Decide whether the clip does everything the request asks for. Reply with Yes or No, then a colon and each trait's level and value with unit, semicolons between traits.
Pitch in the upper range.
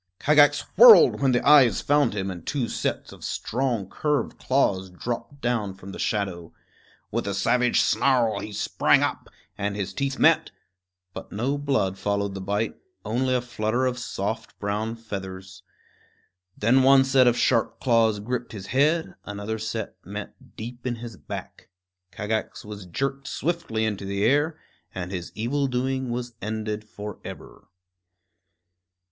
No: low, 115 Hz